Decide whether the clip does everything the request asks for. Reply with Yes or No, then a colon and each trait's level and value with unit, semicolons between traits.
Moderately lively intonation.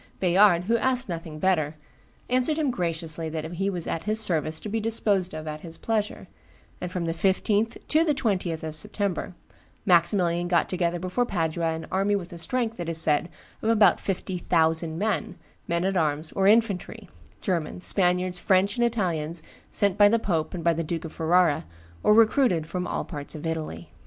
Yes: average, 4.1 semitones